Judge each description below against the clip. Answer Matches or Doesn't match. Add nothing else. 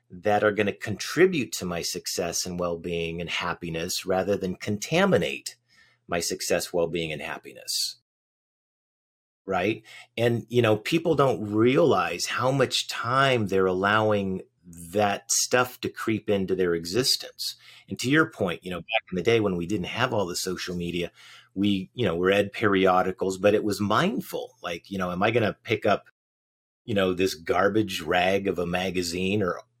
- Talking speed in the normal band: Matches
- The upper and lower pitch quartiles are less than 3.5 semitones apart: Matches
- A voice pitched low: Matches